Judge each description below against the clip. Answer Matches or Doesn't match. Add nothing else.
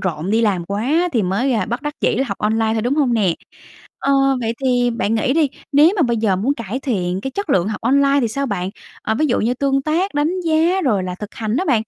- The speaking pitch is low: Doesn't match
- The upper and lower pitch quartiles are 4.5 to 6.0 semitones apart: Matches